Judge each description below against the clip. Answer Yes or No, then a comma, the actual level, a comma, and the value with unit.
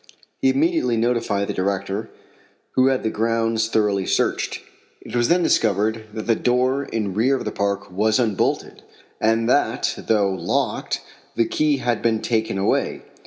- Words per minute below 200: Yes, average, 160 wpm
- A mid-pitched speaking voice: No, low, 115 Hz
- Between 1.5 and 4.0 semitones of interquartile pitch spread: Yes, average, 2.9 semitones